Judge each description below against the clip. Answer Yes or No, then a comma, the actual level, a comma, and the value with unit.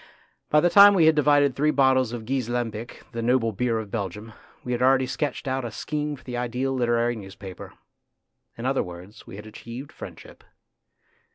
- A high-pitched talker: No, low, 125 Hz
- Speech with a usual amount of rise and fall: Yes, average, 3.2 semitones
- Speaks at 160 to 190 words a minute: Yes, average, 185 wpm